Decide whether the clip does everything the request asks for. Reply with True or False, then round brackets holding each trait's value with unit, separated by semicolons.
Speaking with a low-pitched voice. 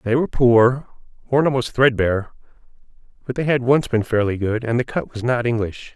True (120 Hz)